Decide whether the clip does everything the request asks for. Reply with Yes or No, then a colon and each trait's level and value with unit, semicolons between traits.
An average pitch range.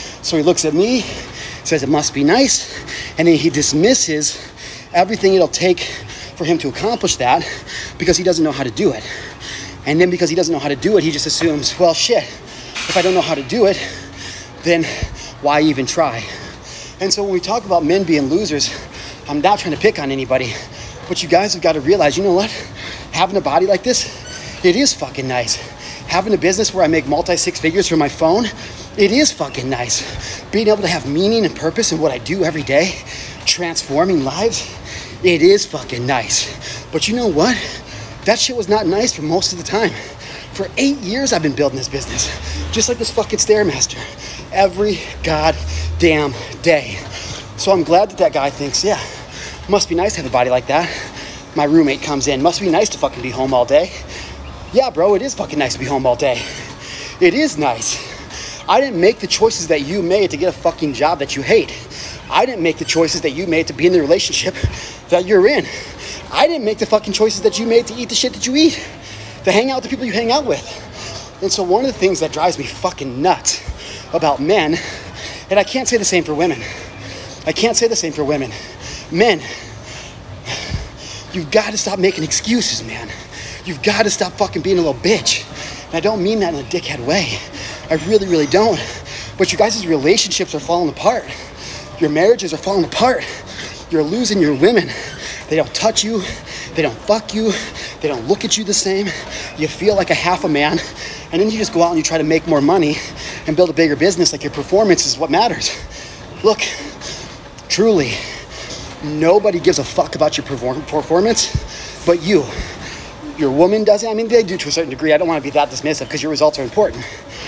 No: wide, 6.7 semitones